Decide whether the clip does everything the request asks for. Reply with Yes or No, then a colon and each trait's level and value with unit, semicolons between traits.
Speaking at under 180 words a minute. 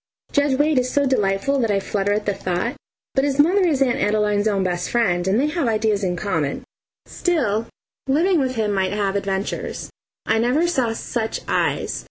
No: average, 190 wpm